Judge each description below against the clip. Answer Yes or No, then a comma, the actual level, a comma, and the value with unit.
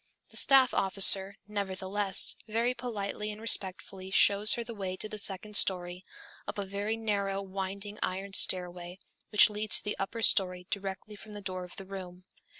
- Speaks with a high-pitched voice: Yes, high, 200 Hz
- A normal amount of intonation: No, narrow, 2.0 semitones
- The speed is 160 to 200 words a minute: Yes, average, 170 wpm